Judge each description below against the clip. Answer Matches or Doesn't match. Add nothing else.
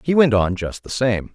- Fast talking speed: Matches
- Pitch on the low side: Matches